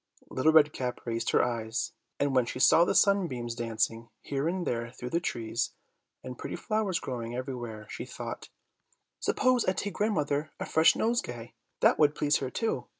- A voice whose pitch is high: No, low, 130 Hz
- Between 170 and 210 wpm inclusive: Yes, average, 175 wpm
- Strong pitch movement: Yes, wide, 5.8 semitones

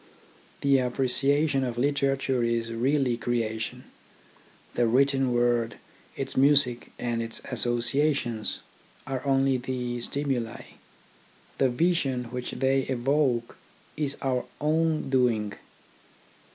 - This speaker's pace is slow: Yes, slow, 100 wpm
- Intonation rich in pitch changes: No, narrow, 2.4 semitones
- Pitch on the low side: Yes, low, 130 Hz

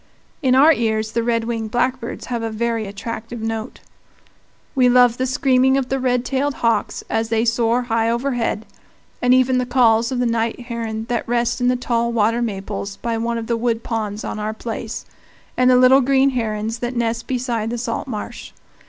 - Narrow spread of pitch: Yes, narrow, 1.8 semitones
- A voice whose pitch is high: Yes, high, 235 Hz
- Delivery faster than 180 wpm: Yes, average, 195 wpm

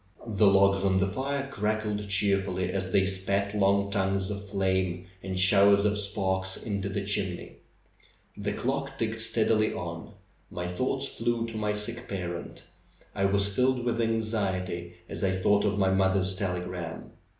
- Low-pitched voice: Yes, low, 100 Hz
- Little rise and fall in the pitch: Yes, narrow, 1.9 semitones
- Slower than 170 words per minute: Yes, average, 155 wpm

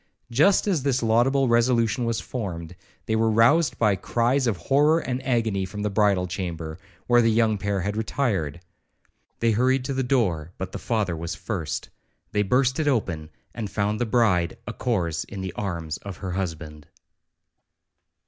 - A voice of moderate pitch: No, low, 110 Hz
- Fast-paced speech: No, average, 170 wpm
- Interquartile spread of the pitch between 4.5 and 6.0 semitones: Yes, average, 5.0 semitones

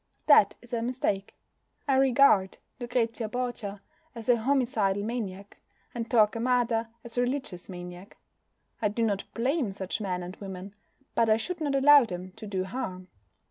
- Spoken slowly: No, average, 155 wpm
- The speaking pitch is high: Yes, high, 225 Hz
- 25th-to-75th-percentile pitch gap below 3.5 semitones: No, average, 4.2 semitones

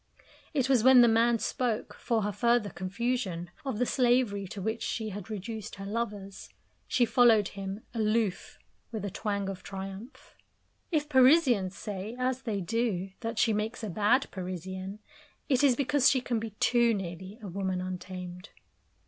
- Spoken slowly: No, average, 165 wpm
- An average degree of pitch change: Yes, average, 3.8 semitones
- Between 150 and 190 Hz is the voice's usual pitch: No, high, 215 Hz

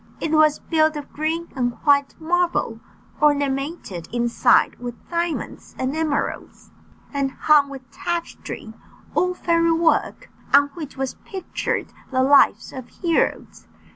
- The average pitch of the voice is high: Yes, very high, 295 Hz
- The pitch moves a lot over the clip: No, average, 3.6 semitones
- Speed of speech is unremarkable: No, slow, 125 wpm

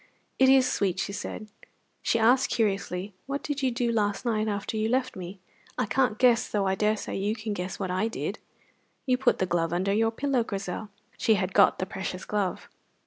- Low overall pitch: No, high, 215 Hz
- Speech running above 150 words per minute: Yes, average, 200 wpm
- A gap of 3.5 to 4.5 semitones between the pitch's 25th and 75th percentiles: Yes, average, 3.8 semitones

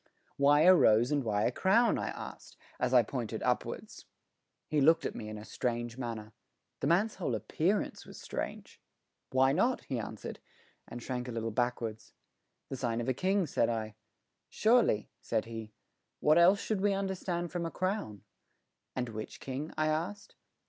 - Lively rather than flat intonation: Yes, wide, 7.9 semitones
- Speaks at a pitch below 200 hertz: Yes, low, 135 Hz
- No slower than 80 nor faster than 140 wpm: No, average, 170 wpm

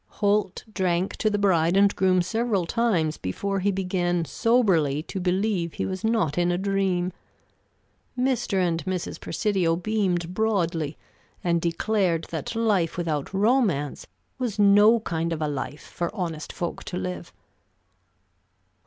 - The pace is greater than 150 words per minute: No, average, 140 wpm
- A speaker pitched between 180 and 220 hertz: Yes, medium, 185 Hz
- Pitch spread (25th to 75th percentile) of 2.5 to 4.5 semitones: Yes, average, 3.4 semitones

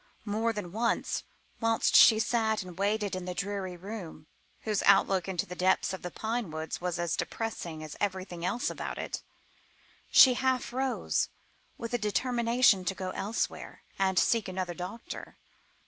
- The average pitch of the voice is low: No, high, 200 Hz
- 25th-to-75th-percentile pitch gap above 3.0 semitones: Yes, average, 3.9 semitones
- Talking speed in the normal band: Yes, average, 160 wpm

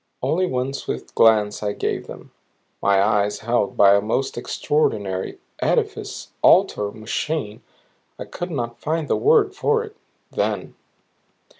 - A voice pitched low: Yes, low, 115 Hz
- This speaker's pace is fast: No, slow, 135 wpm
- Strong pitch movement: Yes, wide, 7.1 semitones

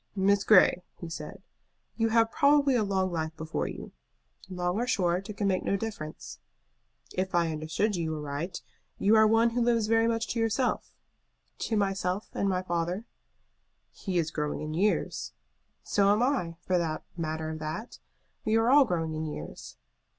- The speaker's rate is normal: Yes, average, 170 wpm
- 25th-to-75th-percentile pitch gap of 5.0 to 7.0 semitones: Yes, average, 5.3 semitones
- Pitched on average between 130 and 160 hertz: No, high, 190 Hz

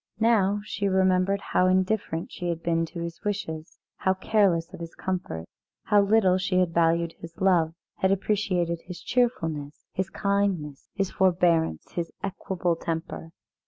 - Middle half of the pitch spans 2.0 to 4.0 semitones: Yes, average, 2.8 semitones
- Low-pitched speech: No, medium, 185 Hz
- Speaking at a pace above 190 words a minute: No, average, 150 wpm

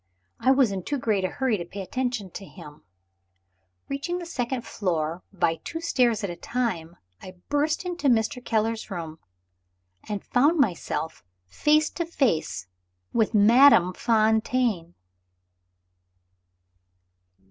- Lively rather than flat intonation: Yes, wide, 6.4 semitones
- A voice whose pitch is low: No, high, 225 Hz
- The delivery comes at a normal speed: No, slow, 130 wpm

